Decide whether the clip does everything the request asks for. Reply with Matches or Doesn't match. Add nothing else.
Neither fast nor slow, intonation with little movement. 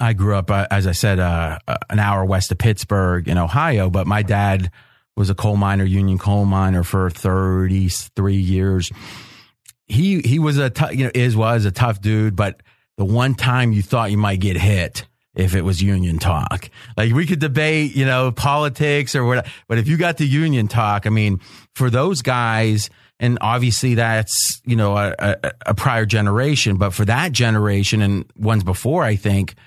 Doesn't match